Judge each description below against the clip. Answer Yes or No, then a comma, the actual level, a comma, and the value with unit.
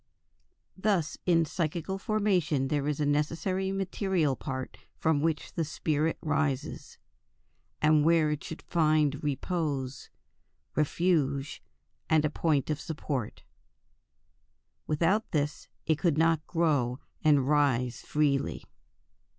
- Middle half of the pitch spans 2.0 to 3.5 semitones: Yes, narrow, 2.6 semitones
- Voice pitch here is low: No, medium, 155 Hz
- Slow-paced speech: Yes, slow, 110 wpm